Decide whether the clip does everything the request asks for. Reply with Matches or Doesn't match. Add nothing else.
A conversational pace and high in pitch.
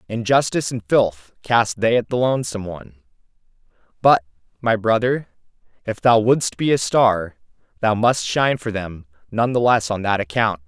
Doesn't match